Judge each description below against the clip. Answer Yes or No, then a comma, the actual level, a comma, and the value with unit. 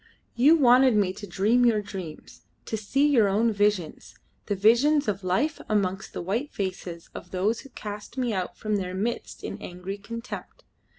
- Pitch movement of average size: Yes, average, 3.9 semitones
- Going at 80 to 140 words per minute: No, average, 175 wpm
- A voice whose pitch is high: Yes, high, 210 Hz